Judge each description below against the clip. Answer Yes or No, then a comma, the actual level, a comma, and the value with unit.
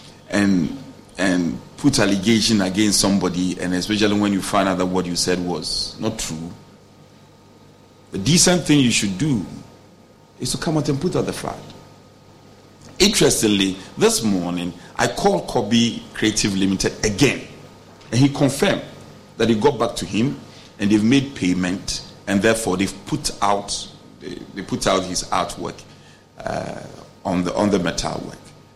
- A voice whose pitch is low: Yes, low, 100 Hz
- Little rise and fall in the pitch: No, average, 3.7 semitones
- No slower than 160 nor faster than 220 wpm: No, average, 150 wpm